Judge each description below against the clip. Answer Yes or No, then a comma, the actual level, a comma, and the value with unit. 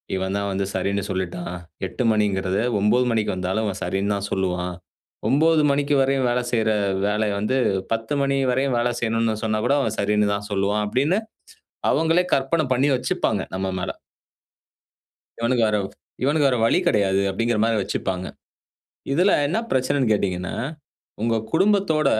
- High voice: No, low, 110 Hz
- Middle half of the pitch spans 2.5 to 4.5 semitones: No, average, 5.2 semitones